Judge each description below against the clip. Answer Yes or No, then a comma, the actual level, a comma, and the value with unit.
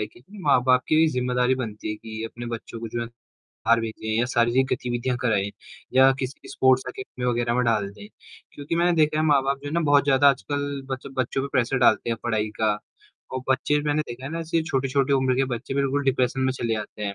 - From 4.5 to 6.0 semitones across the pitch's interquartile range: No, average, 2.9 semitones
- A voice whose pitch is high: No, low, 130 Hz